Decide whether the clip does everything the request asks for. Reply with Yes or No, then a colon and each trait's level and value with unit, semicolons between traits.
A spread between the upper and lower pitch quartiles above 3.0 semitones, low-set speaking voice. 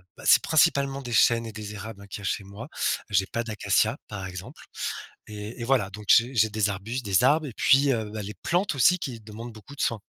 Yes: average, 3.6 semitones; low, 110 Hz